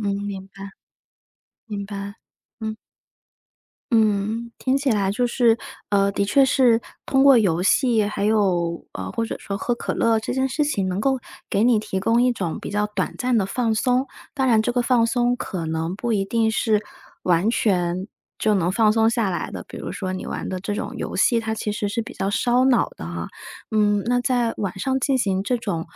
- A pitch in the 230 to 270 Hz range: No, high, 215 Hz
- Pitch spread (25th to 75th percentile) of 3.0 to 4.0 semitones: Yes, average, 3.5 semitones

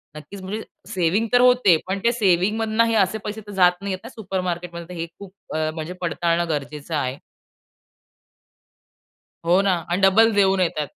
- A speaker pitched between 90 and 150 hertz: No, medium, 185 Hz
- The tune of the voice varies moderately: Yes, average, 3.5 semitones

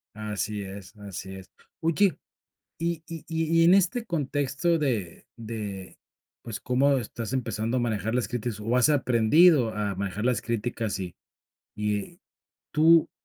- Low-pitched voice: Yes, low, 120 Hz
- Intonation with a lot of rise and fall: Yes, wide, 6.7 semitones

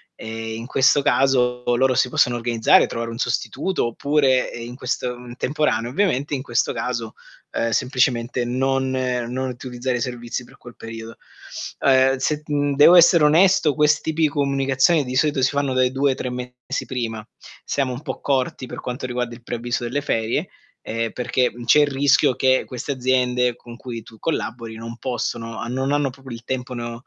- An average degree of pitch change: No, narrow, 2.3 semitones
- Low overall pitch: Yes, low, 125 Hz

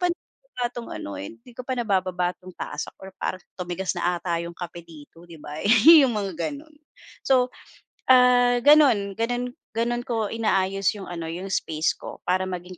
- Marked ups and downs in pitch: Yes, wide, 5.7 semitones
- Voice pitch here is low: No, high, 195 Hz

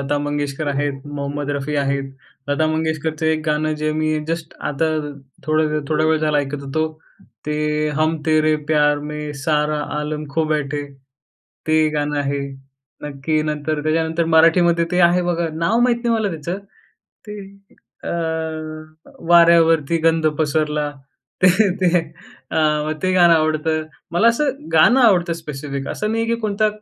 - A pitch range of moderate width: No, narrow, 2.0 semitones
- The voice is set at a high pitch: No, medium, 155 Hz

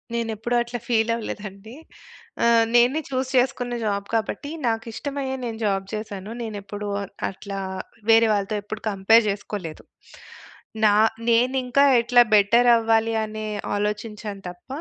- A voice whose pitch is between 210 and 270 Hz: Yes, high, 225 Hz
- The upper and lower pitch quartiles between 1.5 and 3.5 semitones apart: Yes, narrow, 2.6 semitones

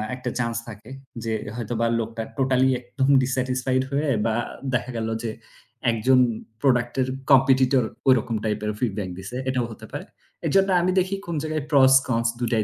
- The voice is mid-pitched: No, low, 125 Hz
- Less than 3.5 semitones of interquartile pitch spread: Yes, narrow, 2.6 semitones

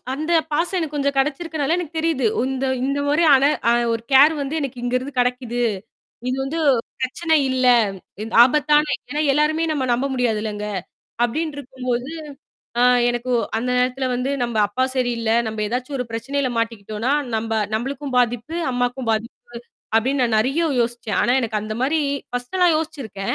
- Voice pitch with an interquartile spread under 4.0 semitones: Yes, average, 3.3 semitones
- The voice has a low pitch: No, very high, 255 Hz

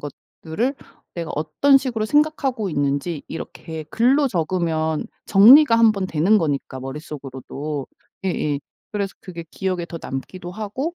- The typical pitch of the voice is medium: Yes, medium, 175 Hz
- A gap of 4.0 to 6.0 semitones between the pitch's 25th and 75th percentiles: No, wide, 6.5 semitones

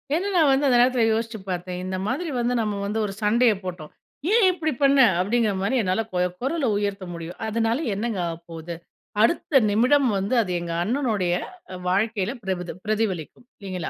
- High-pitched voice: Yes, high, 215 Hz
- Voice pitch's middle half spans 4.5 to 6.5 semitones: Yes, average, 5.2 semitones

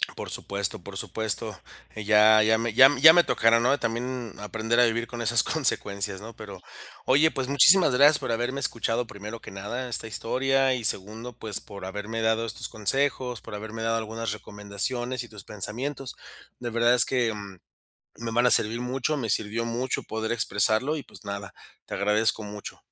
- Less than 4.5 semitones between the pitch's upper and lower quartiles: Yes, average, 2.8 semitones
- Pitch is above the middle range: No, low, 115 Hz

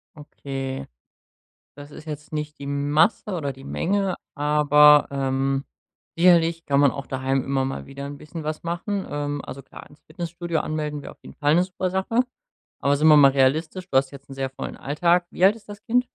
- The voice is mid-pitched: Yes, medium, 150 Hz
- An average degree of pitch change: Yes, average, 3.6 semitones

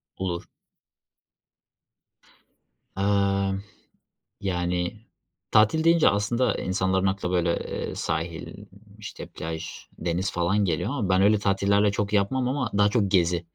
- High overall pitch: No, low, 100 Hz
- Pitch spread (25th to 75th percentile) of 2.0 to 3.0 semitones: Yes, narrow, 2.6 semitones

